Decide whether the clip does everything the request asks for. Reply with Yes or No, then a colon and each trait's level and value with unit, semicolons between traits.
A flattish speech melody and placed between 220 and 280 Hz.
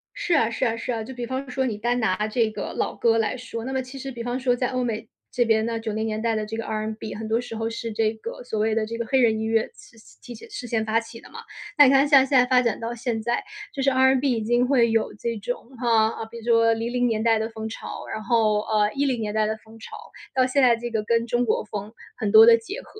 Yes: narrow, 2.1 semitones; high, 230 Hz